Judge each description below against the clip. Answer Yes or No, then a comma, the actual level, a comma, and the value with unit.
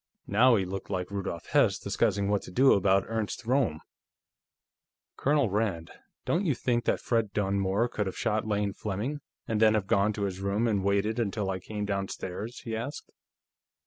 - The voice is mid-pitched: No, low, 105 Hz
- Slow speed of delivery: No, average, 175 wpm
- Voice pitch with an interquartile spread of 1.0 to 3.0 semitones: Yes, average, 2.7 semitones